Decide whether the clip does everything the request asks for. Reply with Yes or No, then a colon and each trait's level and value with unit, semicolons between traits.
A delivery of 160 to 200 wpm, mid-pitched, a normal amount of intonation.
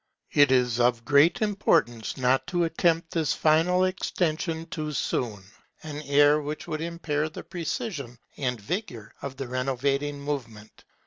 No: average, 140 wpm; medium, 145 Hz; average, 4.4 semitones